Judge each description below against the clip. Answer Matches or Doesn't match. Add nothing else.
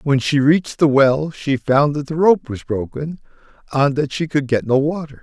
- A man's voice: Matches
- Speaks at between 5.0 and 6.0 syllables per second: Doesn't match